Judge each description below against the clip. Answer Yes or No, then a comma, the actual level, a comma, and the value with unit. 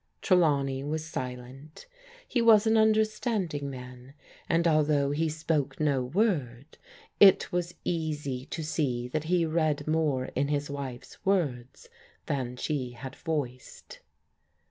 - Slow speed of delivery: Yes, slow, 125 wpm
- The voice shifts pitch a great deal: No, average, 3.9 semitones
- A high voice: No, medium, 150 Hz